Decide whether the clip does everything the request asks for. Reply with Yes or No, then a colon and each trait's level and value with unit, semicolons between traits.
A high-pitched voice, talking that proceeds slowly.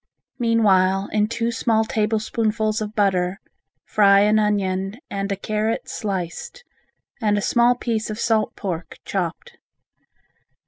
Yes: high, 215 Hz; slow, 125 wpm